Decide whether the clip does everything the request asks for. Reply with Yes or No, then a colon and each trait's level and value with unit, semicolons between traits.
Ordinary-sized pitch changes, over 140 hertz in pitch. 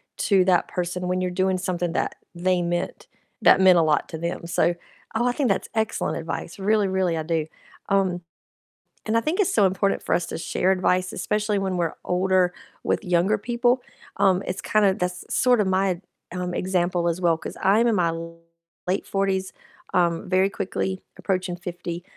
No: narrow, 2.0 semitones; medium, 185 Hz